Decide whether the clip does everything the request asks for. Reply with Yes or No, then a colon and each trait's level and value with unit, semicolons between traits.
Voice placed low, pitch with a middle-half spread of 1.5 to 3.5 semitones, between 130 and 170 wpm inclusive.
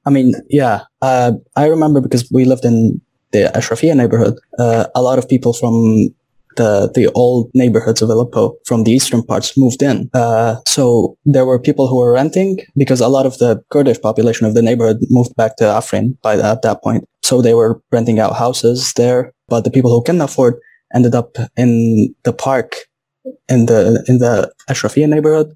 No: low, 125 Hz; narrow, 2.6 semitones; average, 195 wpm